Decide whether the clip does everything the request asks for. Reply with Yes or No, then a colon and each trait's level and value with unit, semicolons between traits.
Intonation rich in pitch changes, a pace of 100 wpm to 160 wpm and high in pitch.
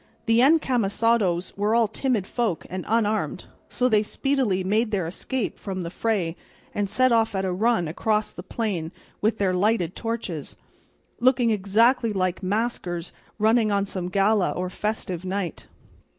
No: average, 3.7 semitones; average, 150 wpm; high, 210 Hz